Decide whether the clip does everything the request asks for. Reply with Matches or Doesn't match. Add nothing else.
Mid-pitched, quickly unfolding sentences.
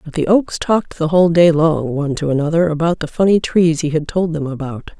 Matches